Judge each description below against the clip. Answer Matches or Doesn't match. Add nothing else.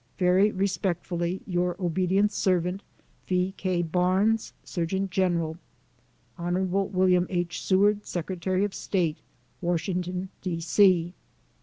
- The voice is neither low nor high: Matches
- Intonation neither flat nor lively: Doesn't match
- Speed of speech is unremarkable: Doesn't match